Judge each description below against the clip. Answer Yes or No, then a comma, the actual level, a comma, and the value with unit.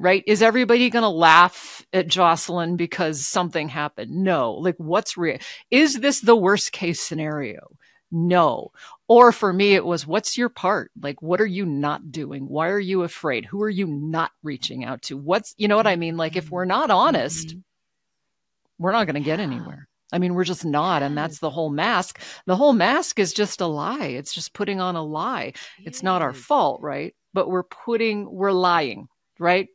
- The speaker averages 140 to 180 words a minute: No, average, 200 wpm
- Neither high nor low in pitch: Yes, medium, 180 Hz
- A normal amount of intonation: Yes, average, 4.1 semitones